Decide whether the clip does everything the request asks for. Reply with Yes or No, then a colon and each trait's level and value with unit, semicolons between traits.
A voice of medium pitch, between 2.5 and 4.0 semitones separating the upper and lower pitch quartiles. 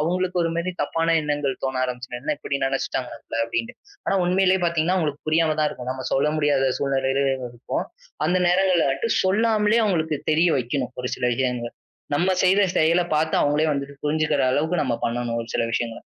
No: medium, 150 Hz; average, 4.5 semitones